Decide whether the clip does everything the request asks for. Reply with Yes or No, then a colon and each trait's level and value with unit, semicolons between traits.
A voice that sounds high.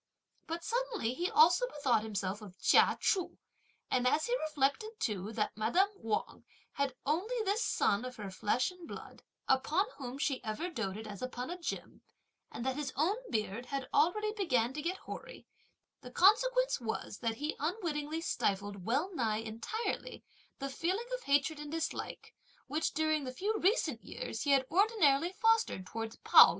Yes: very high, 285 Hz